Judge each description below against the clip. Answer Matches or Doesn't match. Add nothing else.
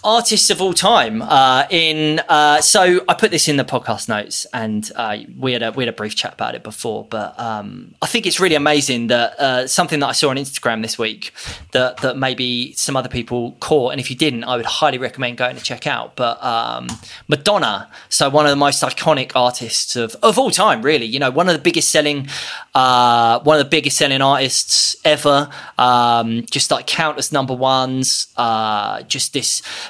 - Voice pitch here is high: Doesn't match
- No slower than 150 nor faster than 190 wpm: Doesn't match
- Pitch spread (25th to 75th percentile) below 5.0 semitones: Matches